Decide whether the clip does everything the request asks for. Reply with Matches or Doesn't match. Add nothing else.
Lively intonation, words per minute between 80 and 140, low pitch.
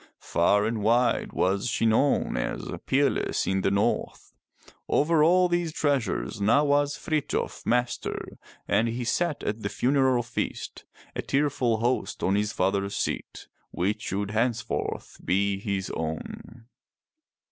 Matches